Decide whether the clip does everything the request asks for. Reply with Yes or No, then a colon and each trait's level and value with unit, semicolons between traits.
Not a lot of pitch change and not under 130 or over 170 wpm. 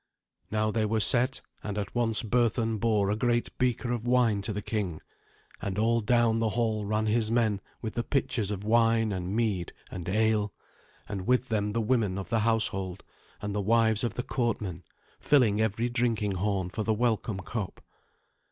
No: narrow, 2.3 semitones; average, 180 wpm